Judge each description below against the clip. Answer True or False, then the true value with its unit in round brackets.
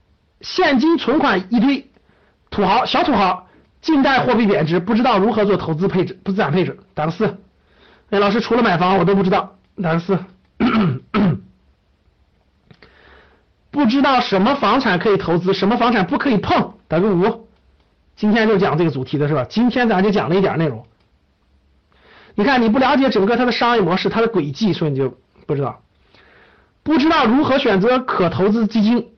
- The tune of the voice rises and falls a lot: False (5.0 semitones)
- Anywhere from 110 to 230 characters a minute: False (270 characters per minute)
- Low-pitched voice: False (200 Hz)